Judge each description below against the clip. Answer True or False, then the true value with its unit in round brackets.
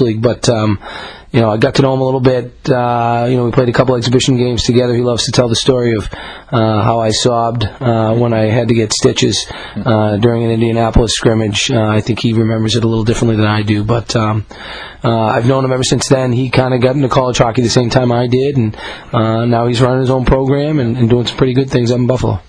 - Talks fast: True (260 wpm)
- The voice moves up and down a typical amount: False (2.2 semitones)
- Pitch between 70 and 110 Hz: False (120 Hz)